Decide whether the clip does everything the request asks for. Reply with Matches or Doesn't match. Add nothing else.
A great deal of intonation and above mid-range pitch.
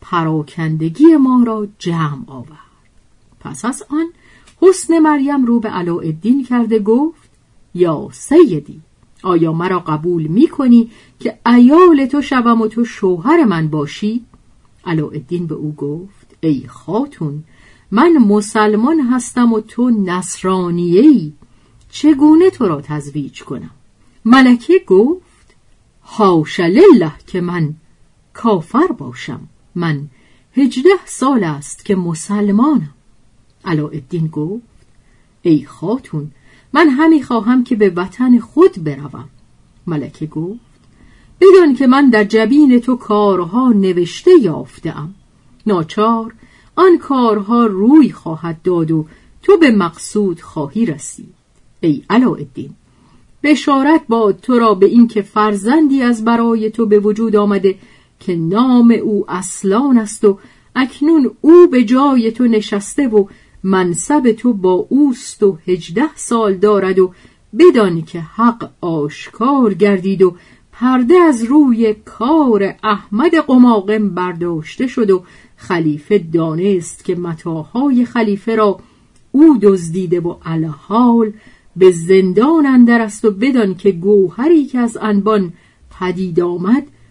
Matches